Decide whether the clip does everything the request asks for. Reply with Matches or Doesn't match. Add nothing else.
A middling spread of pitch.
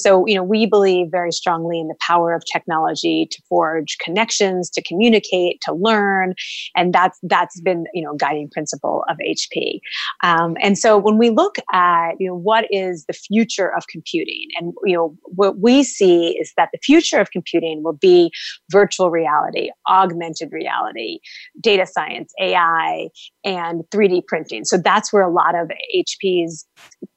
Matches